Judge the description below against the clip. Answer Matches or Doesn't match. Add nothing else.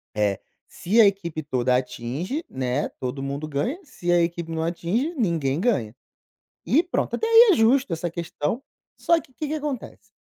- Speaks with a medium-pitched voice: Matches